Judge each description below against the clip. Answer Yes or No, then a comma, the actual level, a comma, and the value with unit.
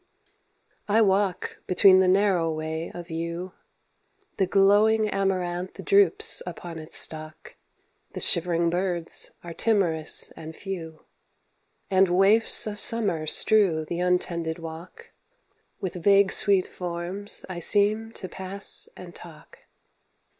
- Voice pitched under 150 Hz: No, medium, 185 Hz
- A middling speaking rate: No, slow, 120 wpm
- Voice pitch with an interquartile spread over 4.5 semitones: No, average, 3.1 semitones